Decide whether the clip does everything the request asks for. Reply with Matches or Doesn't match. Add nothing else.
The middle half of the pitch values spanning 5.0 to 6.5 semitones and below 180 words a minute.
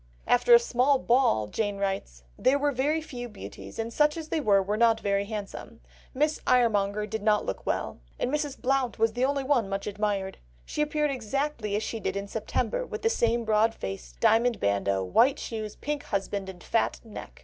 Doesn't match